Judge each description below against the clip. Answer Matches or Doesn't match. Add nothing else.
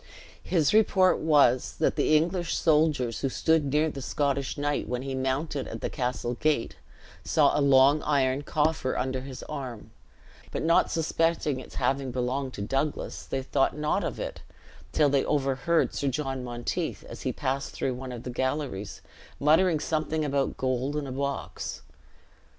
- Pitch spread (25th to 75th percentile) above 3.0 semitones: Doesn't match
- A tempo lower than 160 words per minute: Doesn't match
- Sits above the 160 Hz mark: Doesn't match